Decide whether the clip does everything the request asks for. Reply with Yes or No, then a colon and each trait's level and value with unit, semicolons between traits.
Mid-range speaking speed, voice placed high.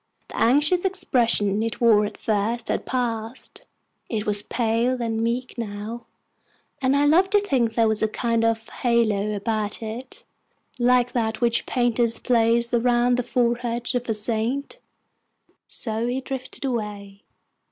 Yes: average, 145 wpm; high, 235 Hz